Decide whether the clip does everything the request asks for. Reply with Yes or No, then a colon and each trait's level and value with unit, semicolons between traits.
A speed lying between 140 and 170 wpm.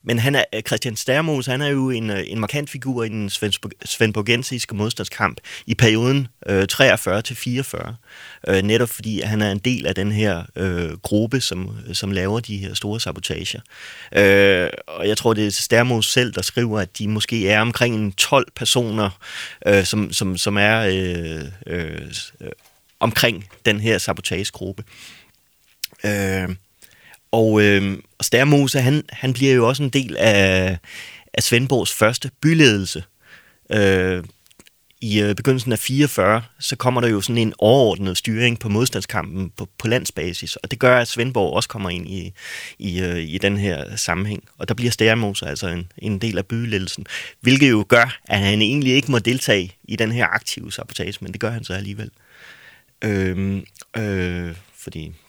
Yes: average, 160 wpm